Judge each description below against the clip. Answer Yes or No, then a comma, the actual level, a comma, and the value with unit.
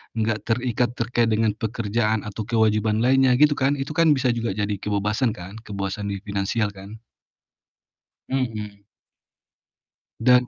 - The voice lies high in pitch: No, low, 110 Hz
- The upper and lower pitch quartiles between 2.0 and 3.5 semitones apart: Yes, average, 2.9 semitones